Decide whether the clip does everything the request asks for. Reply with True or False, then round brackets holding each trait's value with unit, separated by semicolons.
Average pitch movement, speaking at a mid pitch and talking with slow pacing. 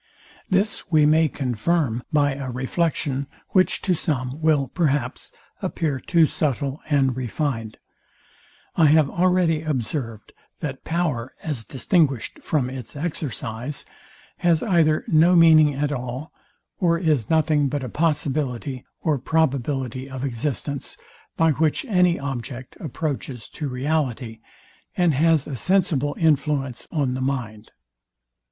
True (3.7 semitones; 145 Hz; 125 wpm)